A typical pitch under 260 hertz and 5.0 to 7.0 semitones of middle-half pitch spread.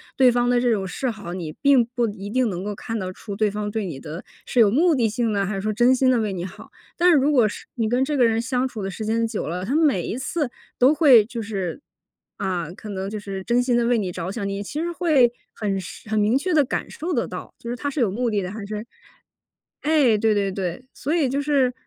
No: high, 225 Hz; average, 4.4 semitones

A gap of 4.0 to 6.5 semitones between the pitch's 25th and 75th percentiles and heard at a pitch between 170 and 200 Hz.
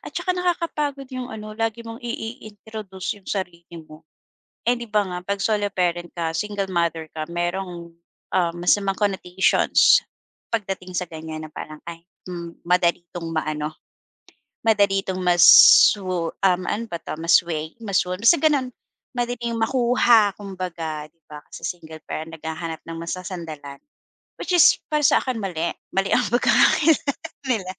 Yes: average, 4.6 semitones; medium, 185 Hz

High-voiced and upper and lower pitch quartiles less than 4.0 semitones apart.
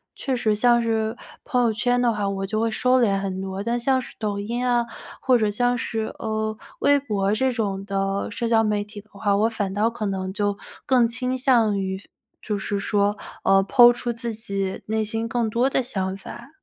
Yes: high, 220 Hz; average, 3.1 semitones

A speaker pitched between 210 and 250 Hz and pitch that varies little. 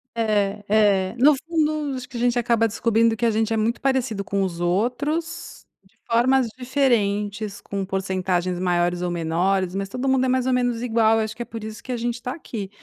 No: high, 225 Hz; average, 4.1 semitones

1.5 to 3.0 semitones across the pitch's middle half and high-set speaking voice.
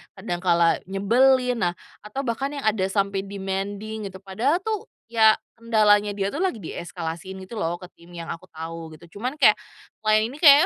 No: average, 4.2 semitones; high, 205 Hz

